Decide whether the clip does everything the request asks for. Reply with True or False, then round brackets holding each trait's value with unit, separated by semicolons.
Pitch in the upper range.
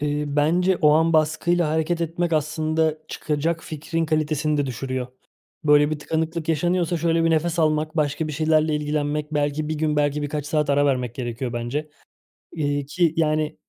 False (155 Hz)